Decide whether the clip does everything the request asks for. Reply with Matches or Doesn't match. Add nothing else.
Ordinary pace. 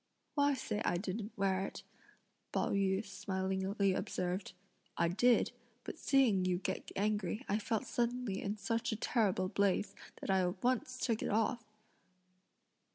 Matches